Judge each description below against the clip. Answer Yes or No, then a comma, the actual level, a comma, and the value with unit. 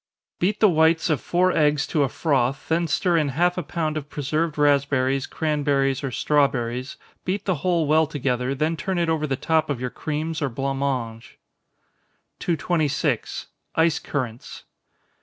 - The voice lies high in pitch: No, medium, 150 Hz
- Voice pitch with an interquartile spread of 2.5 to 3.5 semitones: Yes, average, 3.0 semitones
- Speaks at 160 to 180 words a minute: Yes, average, 165 wpm